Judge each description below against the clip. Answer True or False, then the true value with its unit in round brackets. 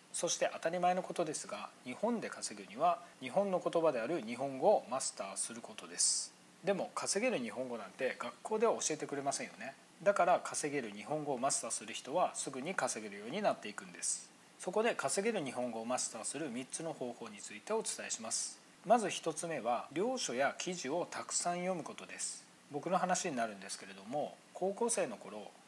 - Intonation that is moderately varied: False (6.0 semitones)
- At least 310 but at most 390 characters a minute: False (410 characters per minute)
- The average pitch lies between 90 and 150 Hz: False (165 Hz)